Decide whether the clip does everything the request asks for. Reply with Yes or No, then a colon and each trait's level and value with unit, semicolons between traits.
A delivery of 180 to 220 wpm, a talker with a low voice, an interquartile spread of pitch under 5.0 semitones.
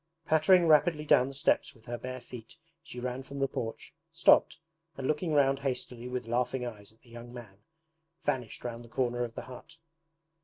Yes: average, 190 wpm; low, 125 Hz; average, 2.7 semitones